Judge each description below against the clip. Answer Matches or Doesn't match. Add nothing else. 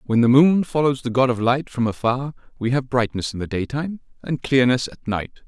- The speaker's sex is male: Matches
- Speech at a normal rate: Doesn't match